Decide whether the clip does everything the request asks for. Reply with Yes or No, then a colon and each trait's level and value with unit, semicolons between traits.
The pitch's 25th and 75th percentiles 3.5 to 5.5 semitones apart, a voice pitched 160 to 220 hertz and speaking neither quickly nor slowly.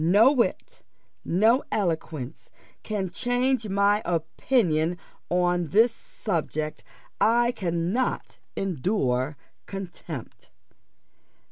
No: average, 5.2 semitones; high, 190 Hz; slow, 80 wpm